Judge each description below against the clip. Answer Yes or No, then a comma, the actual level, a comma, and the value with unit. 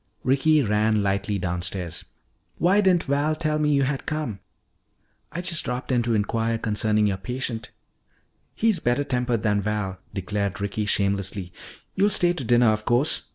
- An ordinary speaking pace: Yes, average, 155 wpm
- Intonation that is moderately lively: No, wide, 5.9 semitones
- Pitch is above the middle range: No, low, 115 Hz